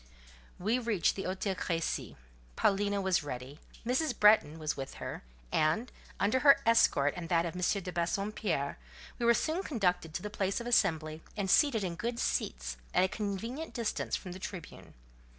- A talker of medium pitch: No, high, 195 Hz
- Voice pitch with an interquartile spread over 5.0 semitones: Yes, wide, 5.5 semitones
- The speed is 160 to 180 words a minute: Yes, average, 170 wpm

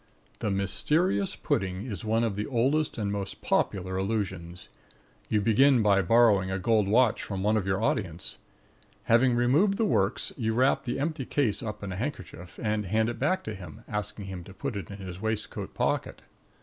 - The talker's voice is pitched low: Yes, low, 105 Hz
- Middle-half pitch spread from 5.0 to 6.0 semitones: No, average, 3.8 semitones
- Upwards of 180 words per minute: Yes, average, 190 wpm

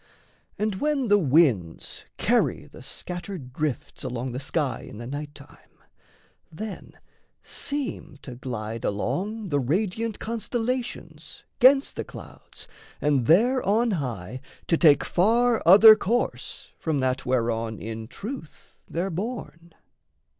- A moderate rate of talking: No, slow, 125 wpm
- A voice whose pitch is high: No, medium, 165 Hz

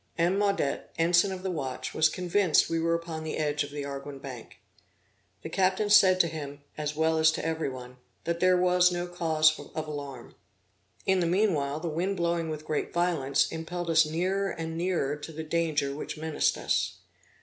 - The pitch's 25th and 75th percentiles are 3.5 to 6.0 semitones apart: No, average, 2.9 semitones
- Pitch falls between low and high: Yes, medium, 160 Hz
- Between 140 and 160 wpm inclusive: No, average, 190 wpm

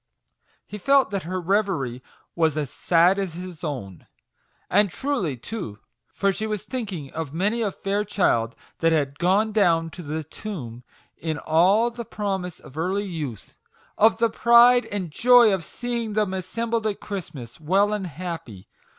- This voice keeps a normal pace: Yes, average, 160 wpm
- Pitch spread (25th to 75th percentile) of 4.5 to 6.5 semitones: Yes, average, 5.1 semitones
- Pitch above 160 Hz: Yes, medium, 185 Hz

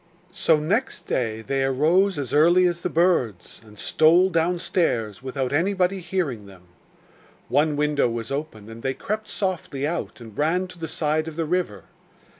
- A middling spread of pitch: No, wide, 5.8 semitones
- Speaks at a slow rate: No, average, 165 wpm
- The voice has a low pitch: No, medium, 155 Hz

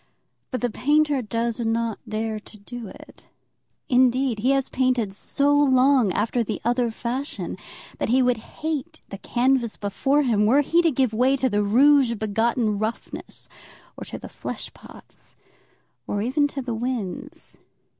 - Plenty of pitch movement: No, average, 3.4 semitones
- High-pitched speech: Yes, high, 245 Hz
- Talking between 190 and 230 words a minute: No, average, 155 wpm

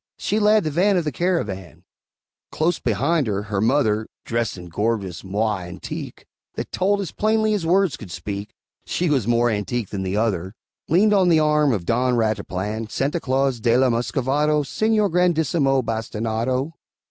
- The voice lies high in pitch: No, low, 125 Hz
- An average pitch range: No, wide, 7.5 semitones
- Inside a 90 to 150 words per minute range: No, average, 165 wpm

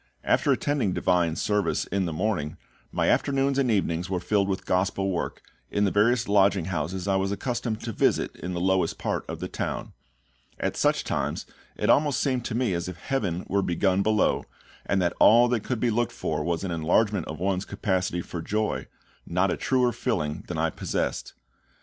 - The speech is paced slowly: No, average, 190 wpm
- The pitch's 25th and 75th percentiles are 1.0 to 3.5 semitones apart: No, average, 4.1 semitones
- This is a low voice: Yes, very low, 95 Hz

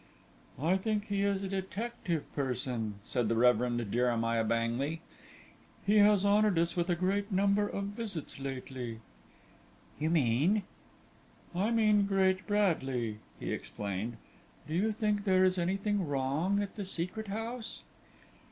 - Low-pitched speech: No, medium, 185 Hz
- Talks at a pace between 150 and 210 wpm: No, average, 140 wpm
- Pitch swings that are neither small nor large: No, wide, 7.7 semitones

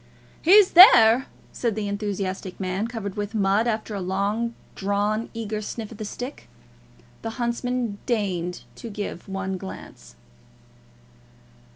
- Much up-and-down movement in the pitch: No, average, 2.9 semitones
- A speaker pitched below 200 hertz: No, high, 210 Hz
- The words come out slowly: Yes, slow, 130 wpm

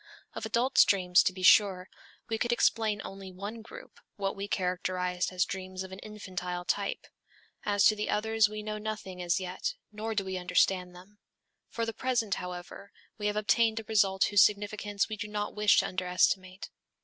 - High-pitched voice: Yes, high, 200 Hz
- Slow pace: No, average, 190 wpm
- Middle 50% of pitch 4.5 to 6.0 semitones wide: No, narrow, 2.5 semitones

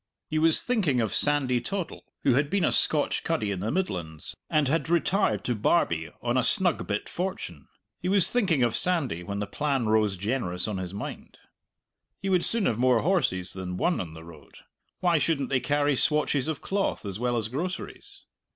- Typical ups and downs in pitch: No, wide, 8.5 semitones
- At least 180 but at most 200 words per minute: Yes, average, 195 wpm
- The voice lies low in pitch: Yes, low, 130 Hz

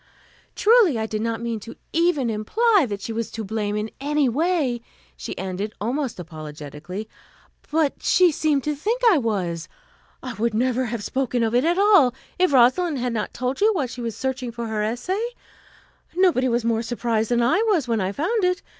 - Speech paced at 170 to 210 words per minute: Yes, average, 190 wpm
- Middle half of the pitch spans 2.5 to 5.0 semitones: No, wide, 5.5 semitones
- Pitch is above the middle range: Yes, high, 240 Hz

